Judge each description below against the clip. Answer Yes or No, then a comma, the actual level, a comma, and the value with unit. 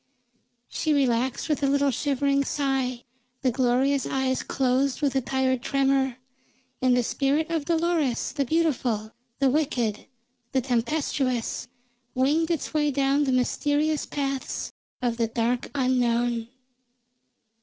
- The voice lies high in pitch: Yes, very high, 270 Hz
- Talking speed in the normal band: No, slow, 125 wpm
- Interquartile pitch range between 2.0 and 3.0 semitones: Yes, narrow, 2.4 semitones